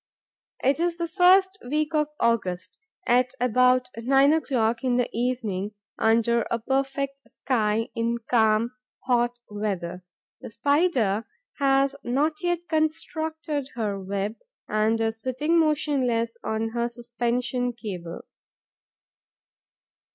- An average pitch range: Yes, average, 4.2 semitones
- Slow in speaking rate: Yes, slow, 115 wpm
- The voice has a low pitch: No, high, 245 Hz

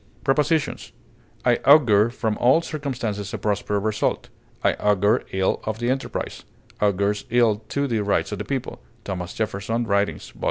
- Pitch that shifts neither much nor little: Yes, average, 3.7 semitones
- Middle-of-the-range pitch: No, low, 110 Hz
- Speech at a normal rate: Yes, average, 155 wpm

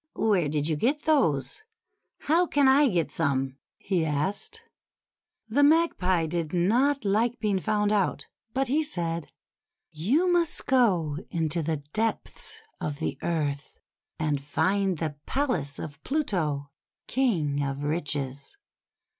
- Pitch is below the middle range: No, medium, 180 Hz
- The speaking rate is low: Yes, slow, 130 wpm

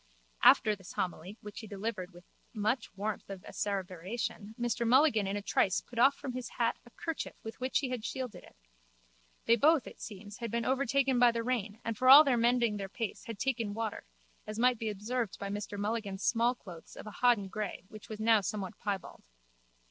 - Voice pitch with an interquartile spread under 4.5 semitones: Yes, average, 3.2 semitones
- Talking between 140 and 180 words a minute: No, average, 200 wpm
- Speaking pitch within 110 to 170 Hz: No, high, 220 Hz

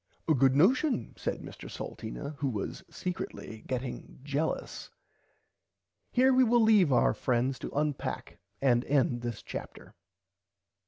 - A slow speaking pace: Yes, slow, 125 wpm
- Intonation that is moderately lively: No, wide, 7.2 semitones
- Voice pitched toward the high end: No, medium, 140 Hz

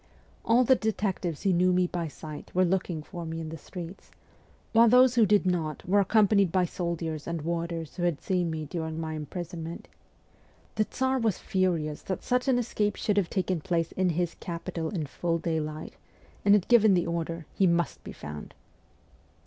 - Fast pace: No, average, 195 wpm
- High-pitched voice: No, medium, 175 Hz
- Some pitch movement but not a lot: Yes, average, 3.5 semitones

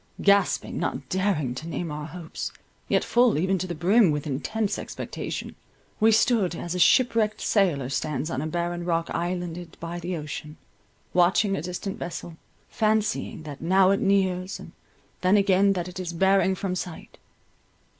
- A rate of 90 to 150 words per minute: No, average, 165 wpm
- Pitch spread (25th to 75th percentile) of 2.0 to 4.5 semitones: Yes, average, 3.0 semitones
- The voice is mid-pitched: Yes, medium, 180 Hz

